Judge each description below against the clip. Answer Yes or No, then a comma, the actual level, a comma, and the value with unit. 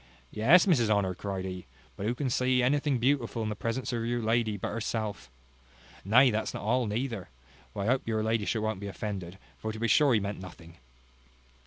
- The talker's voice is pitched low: Yes, low, 110 Hz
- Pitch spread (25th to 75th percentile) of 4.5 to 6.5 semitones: No, average, 3.3 semitones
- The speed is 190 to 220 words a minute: Yes, average, 200 wpm